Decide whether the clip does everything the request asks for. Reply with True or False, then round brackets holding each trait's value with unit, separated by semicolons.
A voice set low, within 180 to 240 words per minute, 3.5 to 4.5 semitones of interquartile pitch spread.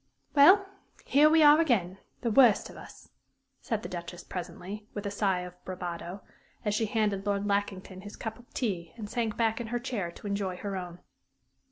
False (205 Hz; 190 wpm; 3.9 semitones)